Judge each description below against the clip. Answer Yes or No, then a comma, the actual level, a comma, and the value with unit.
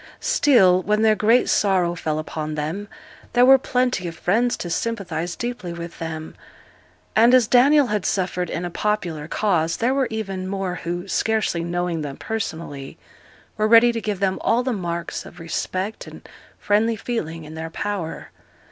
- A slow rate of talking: No, average, 165 wpm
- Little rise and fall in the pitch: No, average, 5.0 semitones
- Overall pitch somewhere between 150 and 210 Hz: Yes, high, 190 Hz